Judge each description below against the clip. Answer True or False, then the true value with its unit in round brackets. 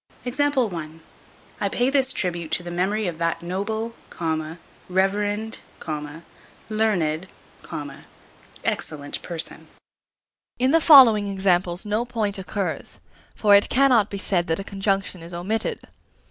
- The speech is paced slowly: True (115 wpm)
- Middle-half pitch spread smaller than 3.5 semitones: False (4.1 semitones)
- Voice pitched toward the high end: True (200 Hz)